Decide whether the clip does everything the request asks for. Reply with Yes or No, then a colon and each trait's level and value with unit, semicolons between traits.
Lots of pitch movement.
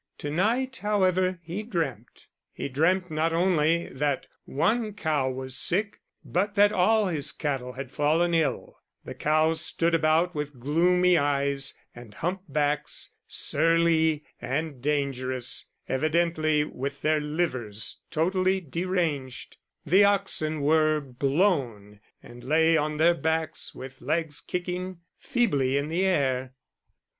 No: average, 4.2 semitones